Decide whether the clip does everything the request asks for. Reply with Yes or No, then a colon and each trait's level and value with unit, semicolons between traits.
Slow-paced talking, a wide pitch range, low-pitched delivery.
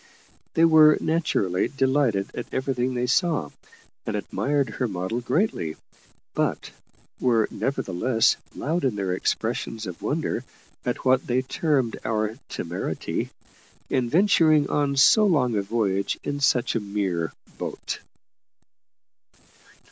Yes: slow, 120 wpm; wide, 5.9 semitones; low, 125 Hz